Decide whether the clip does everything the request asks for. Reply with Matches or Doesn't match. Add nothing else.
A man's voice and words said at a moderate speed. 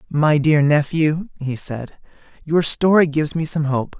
Matches